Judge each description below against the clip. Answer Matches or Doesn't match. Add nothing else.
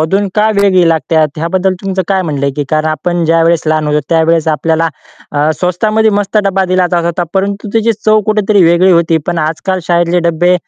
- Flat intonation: Doesn't match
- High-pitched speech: Doesn't match